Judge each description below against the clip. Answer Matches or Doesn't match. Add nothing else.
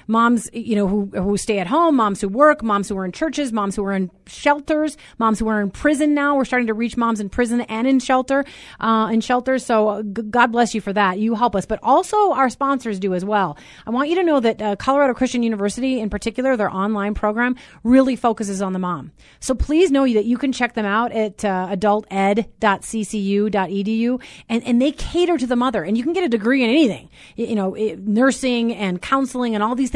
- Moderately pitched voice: Doesn't match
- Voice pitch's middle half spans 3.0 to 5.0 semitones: Matches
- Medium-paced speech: Doesn't match